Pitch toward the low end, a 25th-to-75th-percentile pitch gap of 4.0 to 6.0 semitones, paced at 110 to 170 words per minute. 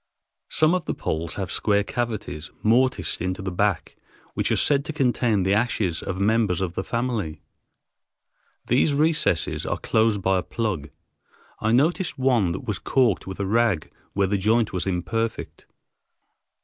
Yes: low, 105 Hz; average, 4.4 semitones; average, 160 wpm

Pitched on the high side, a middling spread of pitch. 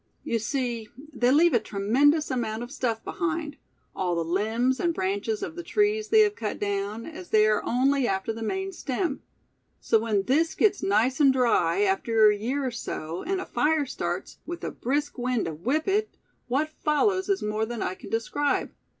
No: very high, 250 Hz; wide, 6.4 semitones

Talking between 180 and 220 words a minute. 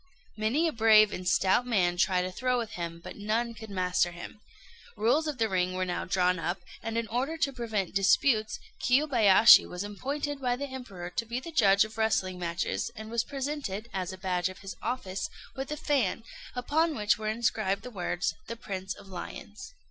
Yes: average, 195 wpm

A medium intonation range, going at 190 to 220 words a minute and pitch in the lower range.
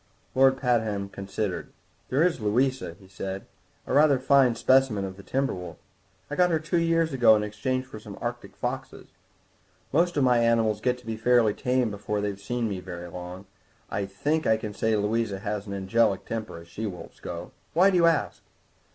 Yes: average, 4.9 semitones; average, 195 wpm; low, 110 Hz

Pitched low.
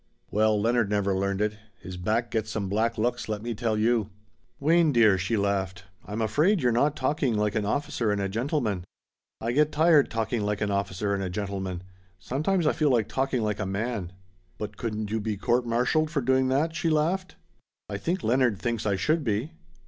Yes: low, 110 Hz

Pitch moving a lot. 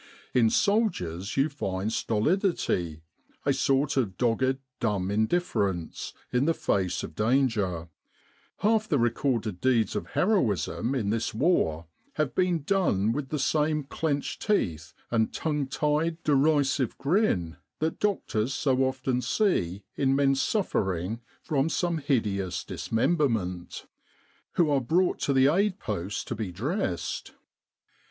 Yes: wide, 7.2 semitones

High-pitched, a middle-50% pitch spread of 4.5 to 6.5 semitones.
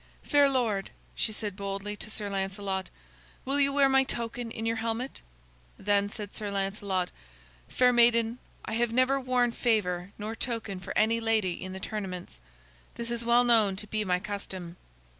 No: high, 215 Hz; average, 3.3 semitones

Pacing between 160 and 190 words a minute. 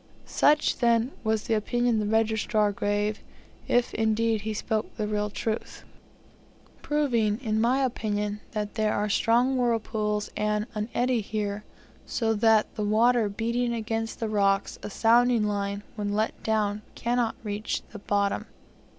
No: average, 145 wpm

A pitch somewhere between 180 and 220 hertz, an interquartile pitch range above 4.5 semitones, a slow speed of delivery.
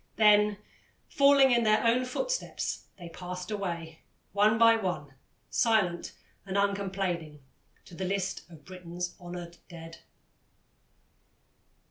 No: high, 190 Hz; average, 3.7 semitones; slow, 110 wpm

